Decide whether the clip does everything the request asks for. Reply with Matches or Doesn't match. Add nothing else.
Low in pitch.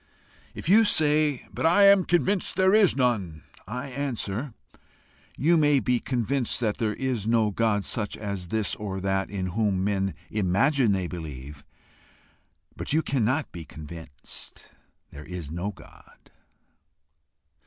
Matches